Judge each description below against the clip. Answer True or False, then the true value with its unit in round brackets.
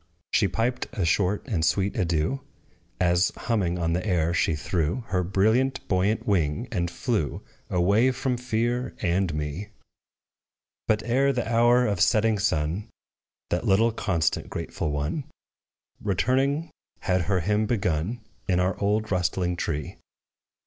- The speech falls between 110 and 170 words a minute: True (135 wpm)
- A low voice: True (100 Hz)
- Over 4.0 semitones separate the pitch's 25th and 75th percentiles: True (4.9 semitones)